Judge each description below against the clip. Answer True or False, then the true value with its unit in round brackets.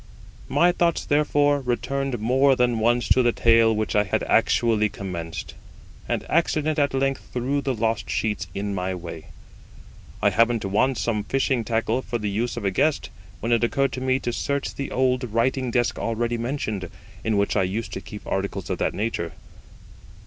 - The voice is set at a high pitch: False (120 Hz)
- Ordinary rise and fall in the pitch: True (4.1 semitones)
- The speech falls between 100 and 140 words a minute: False (185 wpm)